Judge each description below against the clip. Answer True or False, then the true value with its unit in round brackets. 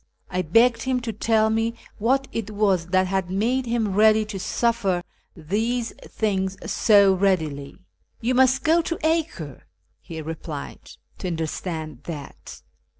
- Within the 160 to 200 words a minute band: False (145 wpm)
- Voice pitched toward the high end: True (205 Hz)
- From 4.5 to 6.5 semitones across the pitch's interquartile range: True (4.8 semitones)